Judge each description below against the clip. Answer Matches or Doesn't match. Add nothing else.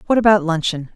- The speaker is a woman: Matches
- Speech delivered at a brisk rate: Doesn't match